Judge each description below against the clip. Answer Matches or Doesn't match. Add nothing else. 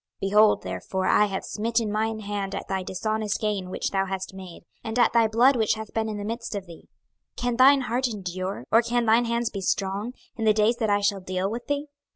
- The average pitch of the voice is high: Matches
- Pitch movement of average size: Matches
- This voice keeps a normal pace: Doesn't match